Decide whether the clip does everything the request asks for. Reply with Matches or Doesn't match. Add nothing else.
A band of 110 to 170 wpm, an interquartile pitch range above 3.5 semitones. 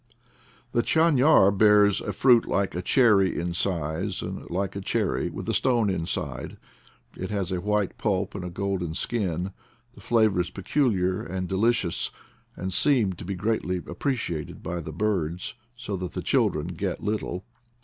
Doesn't match